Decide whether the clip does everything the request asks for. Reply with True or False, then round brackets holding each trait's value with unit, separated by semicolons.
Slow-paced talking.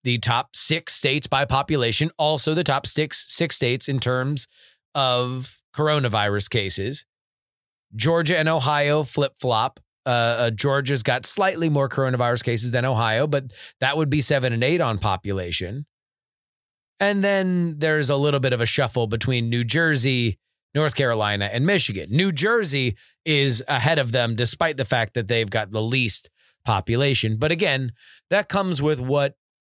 False (160 wpm)